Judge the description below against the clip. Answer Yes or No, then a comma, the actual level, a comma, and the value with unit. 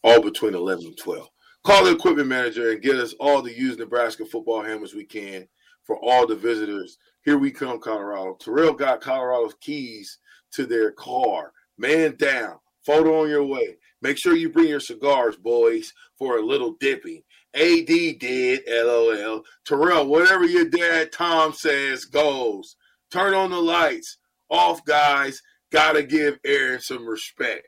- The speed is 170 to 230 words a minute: No, average, 160 wpm